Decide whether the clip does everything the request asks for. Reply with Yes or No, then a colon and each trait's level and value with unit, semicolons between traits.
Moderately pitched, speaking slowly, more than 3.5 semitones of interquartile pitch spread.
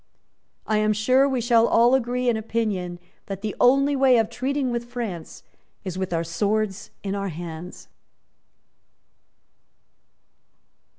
No: high, 220 Hz; slow, 130 wpm; average, 4.2 semitones